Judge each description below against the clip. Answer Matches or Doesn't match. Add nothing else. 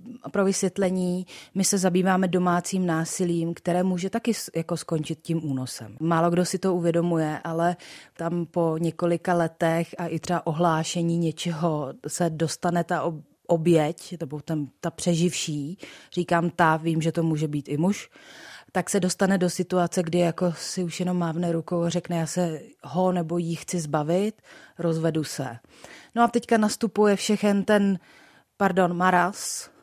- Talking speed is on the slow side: Doesn't match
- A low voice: Doesn't match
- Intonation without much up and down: Matches